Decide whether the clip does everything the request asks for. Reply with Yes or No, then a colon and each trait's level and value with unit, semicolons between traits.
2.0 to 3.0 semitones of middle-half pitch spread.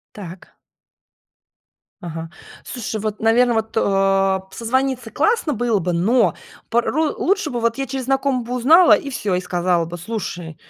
No: wide, 5.6 semitones